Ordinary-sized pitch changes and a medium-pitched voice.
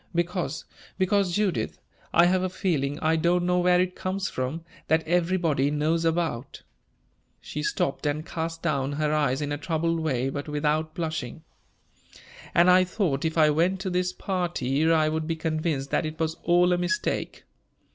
Yes: average, 3.0 semitones; medium, 160 Hz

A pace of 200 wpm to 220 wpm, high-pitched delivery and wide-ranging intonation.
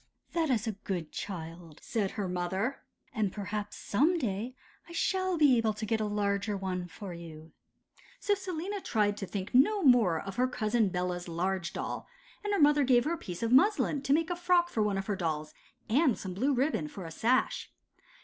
Yes: fast, 205 wpm; high, 215 Hz; wide, 6.9 semitones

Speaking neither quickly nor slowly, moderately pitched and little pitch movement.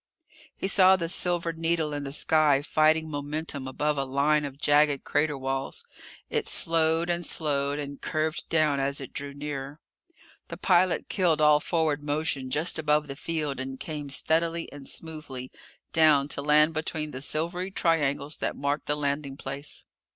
Yes: average, 165 wpm; medium, 150 Hz; narrow, 2.3 semitones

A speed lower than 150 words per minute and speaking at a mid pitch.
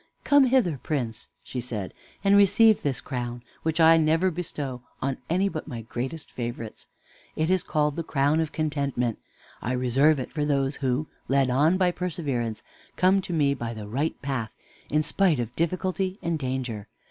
No: average, 170 wpm; medium, 145 Hz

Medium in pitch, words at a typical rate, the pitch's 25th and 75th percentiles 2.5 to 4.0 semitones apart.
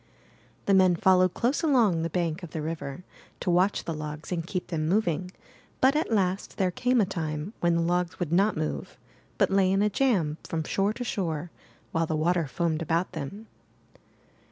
Yes: medium, 175 Hz; average, 190 wpm; average, 3.5 semitones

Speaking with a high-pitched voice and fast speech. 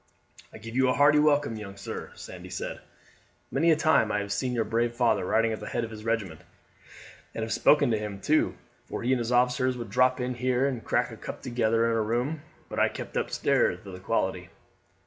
No: low, 115 Hz; fast, 220 wpm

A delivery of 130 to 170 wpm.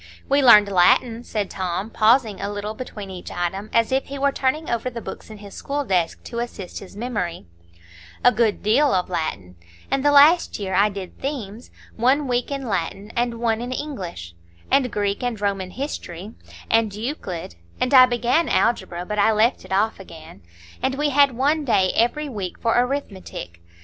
No: average, 180 wpm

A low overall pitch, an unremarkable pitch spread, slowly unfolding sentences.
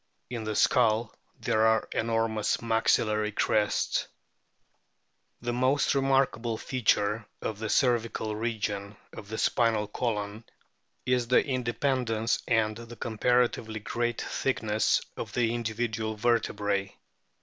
No: low, 115 Hz; narrow, 1.9 semitones; slow, 110 wpm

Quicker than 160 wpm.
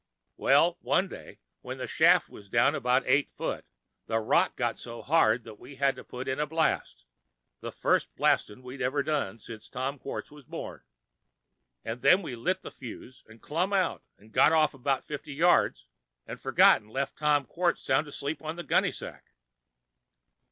Yes: average, 175 wpm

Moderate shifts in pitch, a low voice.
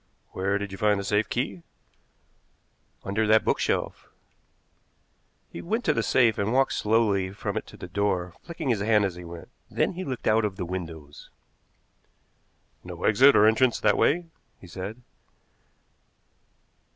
Yes: average, 3.9 semitones; low, 105 Hz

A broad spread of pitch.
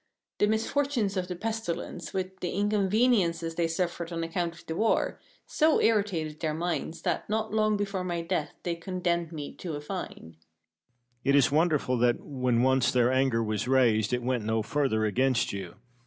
Yes: wide, 6.5 semitones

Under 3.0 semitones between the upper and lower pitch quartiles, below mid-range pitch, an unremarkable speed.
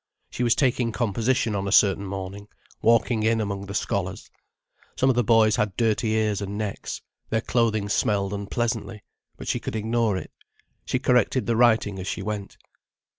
Yes: narrow, 2.5 semitones; low, 110 Hz; average, 175 wpm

